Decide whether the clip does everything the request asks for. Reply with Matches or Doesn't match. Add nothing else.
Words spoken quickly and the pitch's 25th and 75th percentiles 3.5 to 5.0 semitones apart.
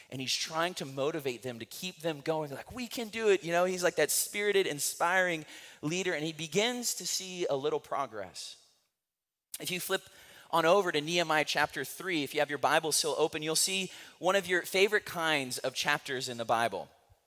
Matches